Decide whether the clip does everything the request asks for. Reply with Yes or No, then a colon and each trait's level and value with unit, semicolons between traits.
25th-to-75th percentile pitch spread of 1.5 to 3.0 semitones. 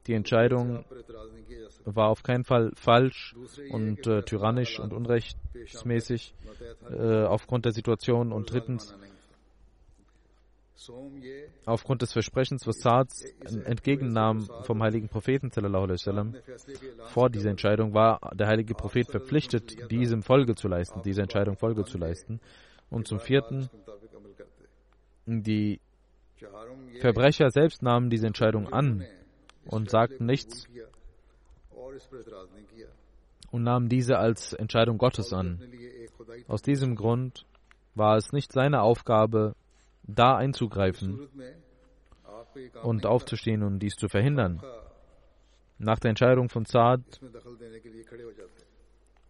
Yes: narrow, 2.4 semitones